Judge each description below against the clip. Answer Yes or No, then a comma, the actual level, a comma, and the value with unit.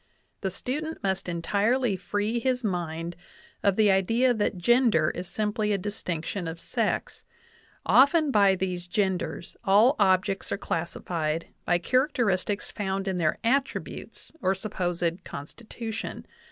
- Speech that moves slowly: Yes, slow, 130 wpm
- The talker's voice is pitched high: Yes, high, 195 Hz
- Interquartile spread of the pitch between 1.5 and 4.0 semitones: No, average, 4.4 semitones